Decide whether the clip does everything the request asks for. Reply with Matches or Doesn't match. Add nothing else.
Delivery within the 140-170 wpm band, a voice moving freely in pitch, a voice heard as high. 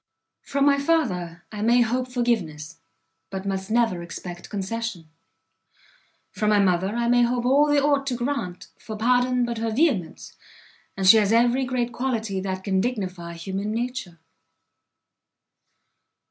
Doesn't match